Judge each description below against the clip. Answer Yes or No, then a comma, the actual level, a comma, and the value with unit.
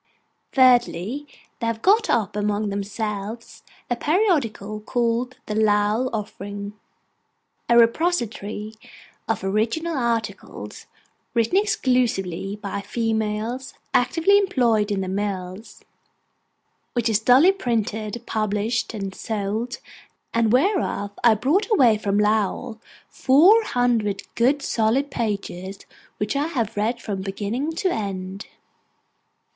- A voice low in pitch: No, high, 225 Hz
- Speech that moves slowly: Yes, slow, 110 wpm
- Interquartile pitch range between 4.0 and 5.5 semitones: No, average, 3.5 semitones